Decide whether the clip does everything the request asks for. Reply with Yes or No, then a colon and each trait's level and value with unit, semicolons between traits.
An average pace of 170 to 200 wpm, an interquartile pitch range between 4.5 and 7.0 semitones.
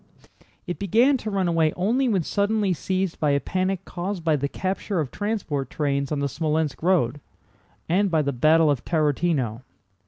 Yes: average, 175 wpm; average, 4.8 semitones